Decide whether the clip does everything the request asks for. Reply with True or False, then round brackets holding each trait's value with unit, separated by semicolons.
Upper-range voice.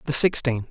False (135 Hz)